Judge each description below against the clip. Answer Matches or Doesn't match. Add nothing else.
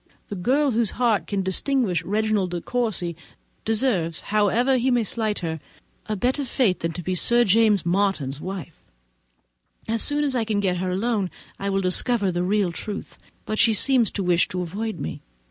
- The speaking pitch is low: Doesn't match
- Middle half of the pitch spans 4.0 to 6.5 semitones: Matches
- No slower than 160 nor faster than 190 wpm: Matches